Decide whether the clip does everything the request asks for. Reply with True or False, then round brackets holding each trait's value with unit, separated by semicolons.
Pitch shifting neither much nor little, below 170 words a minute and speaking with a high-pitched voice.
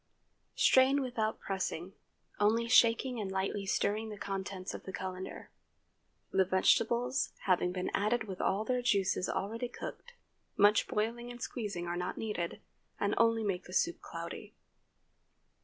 True (3.6 semitones; 140 wpm; 210 Hz)